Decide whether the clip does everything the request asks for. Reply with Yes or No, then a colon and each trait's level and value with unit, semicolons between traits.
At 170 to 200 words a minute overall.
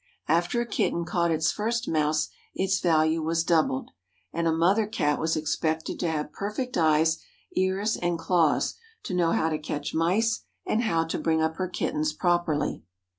Yes: average, 175 wpm